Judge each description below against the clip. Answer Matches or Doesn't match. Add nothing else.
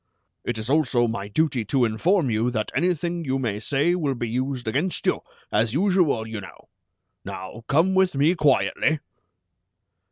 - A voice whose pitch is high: Doesn't match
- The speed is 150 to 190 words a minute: Matches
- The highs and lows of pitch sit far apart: Matches